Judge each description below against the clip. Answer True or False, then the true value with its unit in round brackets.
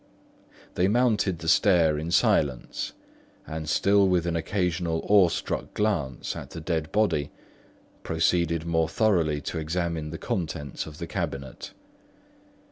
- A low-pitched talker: True (85 Hz)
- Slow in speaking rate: True (125 wpm)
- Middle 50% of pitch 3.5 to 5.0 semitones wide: False (2.8 semitones)